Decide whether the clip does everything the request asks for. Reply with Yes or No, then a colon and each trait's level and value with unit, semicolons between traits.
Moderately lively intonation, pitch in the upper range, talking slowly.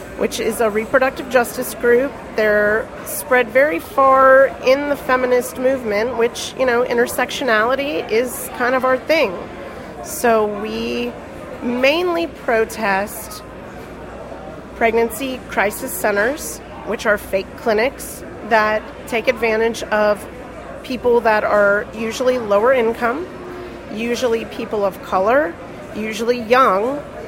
Yes: average, 3.0 semitones; high, 240 Hz; slow, 110 wpm